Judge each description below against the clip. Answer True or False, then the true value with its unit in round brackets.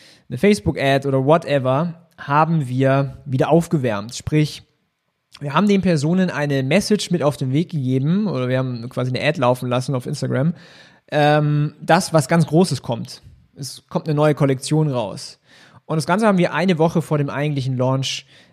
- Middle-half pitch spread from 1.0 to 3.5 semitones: False (3.9 semitones)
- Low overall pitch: False (150 Hz)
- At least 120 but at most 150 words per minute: False (170 wpm)